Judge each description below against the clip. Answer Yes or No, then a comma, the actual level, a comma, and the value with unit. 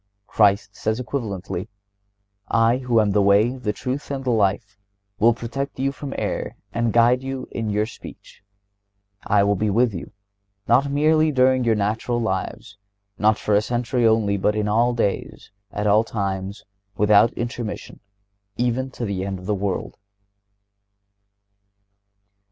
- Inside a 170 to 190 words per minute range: No, average, 150 wpm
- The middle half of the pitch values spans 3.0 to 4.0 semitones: Yes, average, 3.4 semitones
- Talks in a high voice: No, low, 110 Hz